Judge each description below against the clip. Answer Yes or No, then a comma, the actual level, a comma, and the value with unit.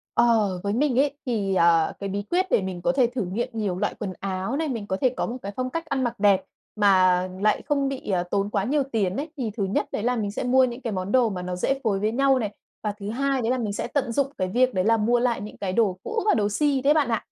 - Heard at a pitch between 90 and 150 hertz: No, high, 225 Hz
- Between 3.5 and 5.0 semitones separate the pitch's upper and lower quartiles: Yes, average, 4.6 semitones